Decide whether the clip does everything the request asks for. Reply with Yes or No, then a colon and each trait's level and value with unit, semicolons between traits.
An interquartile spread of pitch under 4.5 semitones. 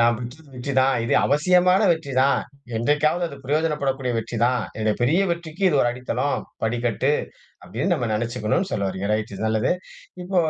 No: average, 4.8 semitones